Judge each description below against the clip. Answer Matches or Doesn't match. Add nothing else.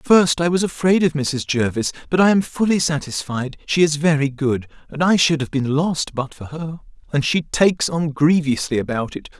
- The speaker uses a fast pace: Matches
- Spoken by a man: Matches